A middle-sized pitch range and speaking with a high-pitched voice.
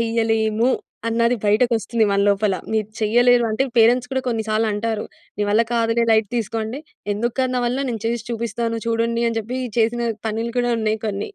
No: narrow, 1.4 semitones; high, 230 Hz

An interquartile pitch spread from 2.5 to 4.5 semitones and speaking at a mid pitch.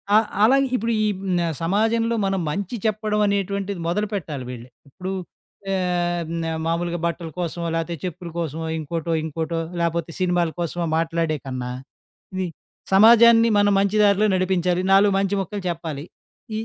Yes: average, 3.3 semitones; medium, 180 Hz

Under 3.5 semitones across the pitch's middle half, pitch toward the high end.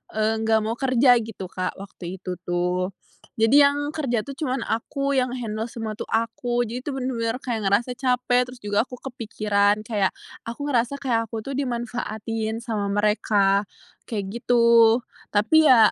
Yes: average, 3.0 semitones; high, 230 Hz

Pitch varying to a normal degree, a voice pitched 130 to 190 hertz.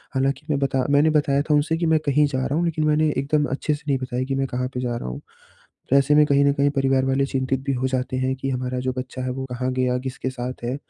No: narrow, 2.0 semitones; low, 135 Hz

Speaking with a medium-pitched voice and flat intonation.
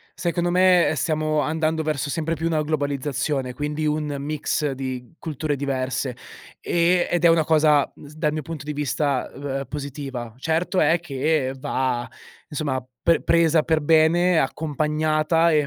Yes: medium, 150 Hz; narrow, 2.3 semitones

